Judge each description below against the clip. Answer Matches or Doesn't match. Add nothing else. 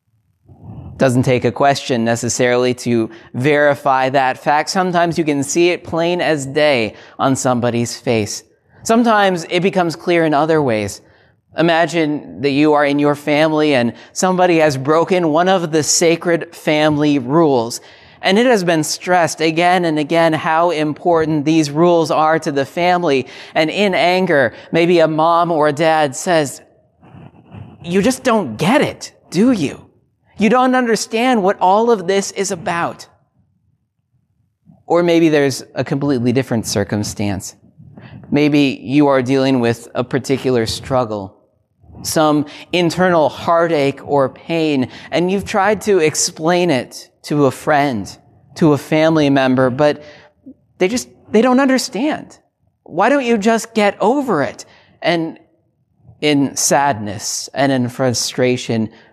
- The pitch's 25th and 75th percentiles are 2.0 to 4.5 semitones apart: Doesn't match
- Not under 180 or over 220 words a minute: Doesn't match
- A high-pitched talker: Doesn't match